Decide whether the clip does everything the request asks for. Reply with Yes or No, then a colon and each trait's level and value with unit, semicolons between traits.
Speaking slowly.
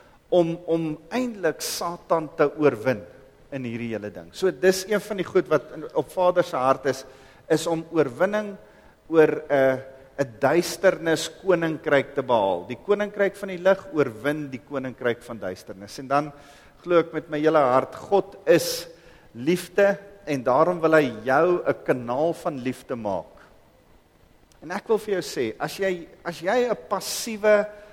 No: average, 165 wpm